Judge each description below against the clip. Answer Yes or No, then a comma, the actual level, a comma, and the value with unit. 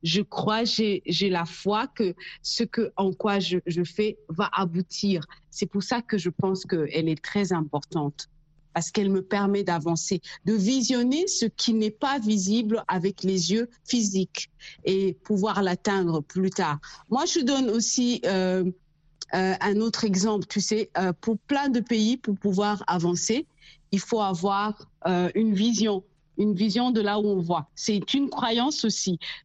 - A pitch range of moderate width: Yes, average, 3.4 semitones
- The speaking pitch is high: Yes, high, 200 Hz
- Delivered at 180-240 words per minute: No, average, 170 wpm